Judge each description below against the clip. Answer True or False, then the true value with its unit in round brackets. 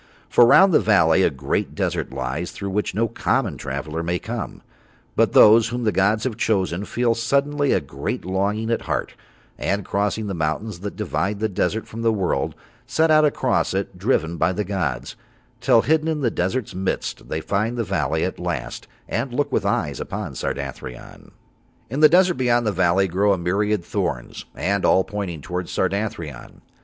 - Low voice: True (105 Hz)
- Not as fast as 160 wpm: False (180 wpm)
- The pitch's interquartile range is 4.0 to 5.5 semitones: True (4.4 semitones)